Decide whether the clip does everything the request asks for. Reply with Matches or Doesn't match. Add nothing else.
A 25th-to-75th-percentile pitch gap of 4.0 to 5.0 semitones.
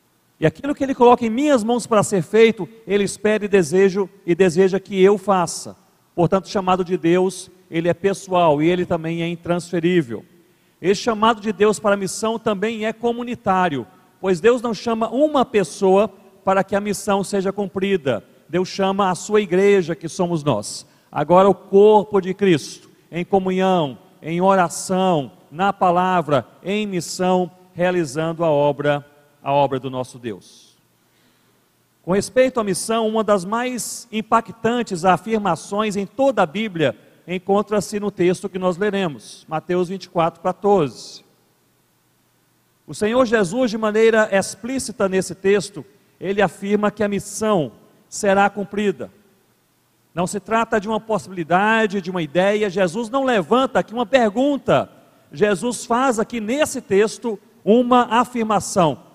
Doesn't match